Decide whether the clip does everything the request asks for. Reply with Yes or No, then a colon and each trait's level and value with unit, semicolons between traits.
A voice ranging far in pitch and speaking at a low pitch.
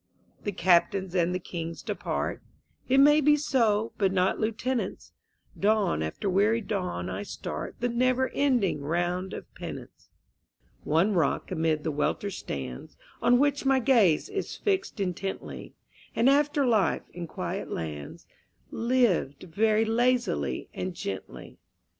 No: wide, 6.3 semitones; high, 200 Hz